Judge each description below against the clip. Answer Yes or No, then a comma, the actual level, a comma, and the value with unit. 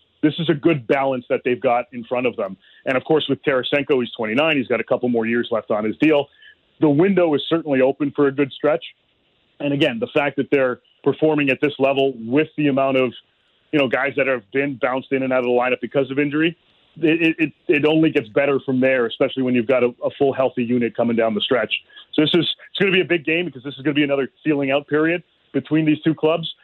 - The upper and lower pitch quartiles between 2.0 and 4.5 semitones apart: Yes, average, 3.2 semitones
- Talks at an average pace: No, fast, 255 wpm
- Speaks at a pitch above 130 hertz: Yes, medium, 140 Hz